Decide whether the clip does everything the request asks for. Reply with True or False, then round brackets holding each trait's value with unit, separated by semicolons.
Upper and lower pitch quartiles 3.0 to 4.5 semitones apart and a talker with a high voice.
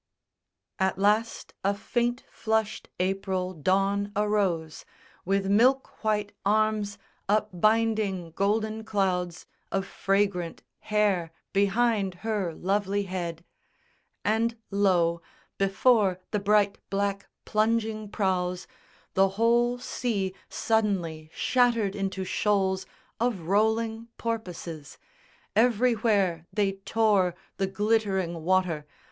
False (2.6 semitones; 200 Hz)